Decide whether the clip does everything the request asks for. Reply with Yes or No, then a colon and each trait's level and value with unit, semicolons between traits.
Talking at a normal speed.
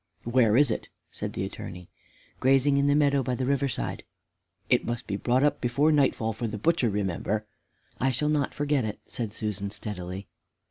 Yes: average, 185 wpm